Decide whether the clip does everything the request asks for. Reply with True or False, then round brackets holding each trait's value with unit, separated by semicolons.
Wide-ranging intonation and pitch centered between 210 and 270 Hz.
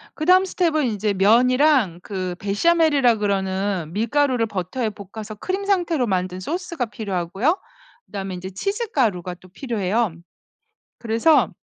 True (7.3 semitones; 220 Hz)